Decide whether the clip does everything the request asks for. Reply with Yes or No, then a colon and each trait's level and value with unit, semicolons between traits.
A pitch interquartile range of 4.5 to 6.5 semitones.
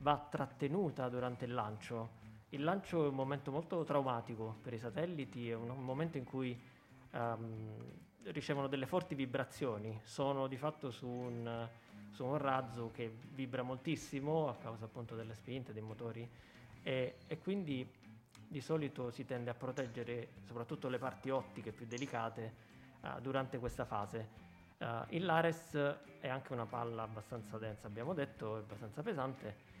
No: average, 3.5 semitones